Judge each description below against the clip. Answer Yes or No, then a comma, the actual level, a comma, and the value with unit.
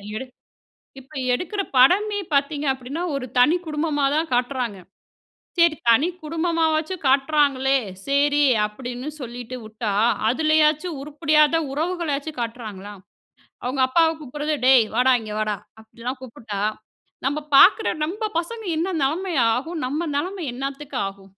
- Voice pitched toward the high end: Yes, very high, 280 Hz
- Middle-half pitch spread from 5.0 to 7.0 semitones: No, average, 4.3 semitones